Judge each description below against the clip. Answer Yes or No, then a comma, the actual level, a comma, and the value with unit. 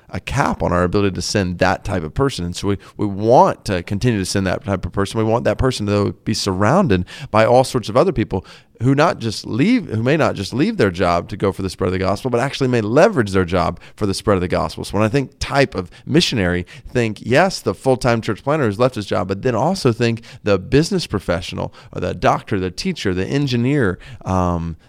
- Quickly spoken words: Yes, fast, 240 wpm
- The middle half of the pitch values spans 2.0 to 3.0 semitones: No, average, 5.3 semitones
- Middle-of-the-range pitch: No, low, 105 Hz